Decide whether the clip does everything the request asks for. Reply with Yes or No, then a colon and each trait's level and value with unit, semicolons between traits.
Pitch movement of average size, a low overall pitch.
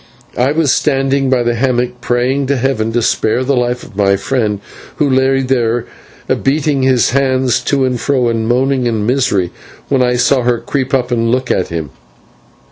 No: narrow, 2.1 semitones; low, 125 Hz